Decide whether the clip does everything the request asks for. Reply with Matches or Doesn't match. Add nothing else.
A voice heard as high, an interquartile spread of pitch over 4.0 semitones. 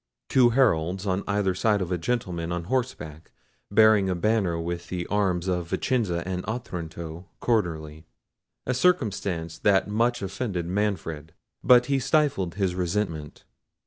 Doesn't match